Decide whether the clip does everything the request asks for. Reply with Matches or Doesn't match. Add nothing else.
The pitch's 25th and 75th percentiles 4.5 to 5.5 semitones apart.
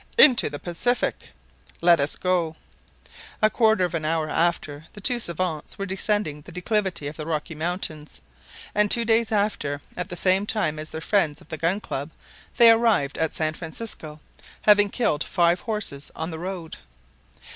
Matches